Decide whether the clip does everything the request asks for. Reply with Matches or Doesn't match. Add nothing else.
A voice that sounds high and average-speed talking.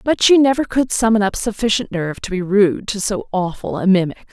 Doesn't match